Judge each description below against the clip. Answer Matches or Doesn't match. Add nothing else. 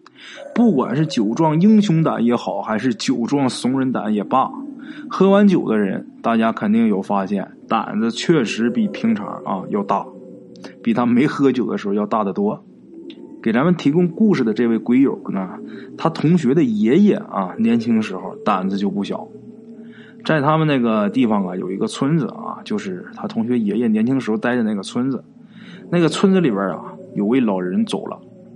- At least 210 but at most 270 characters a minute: Matches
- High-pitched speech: Matches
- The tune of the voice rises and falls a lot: Matches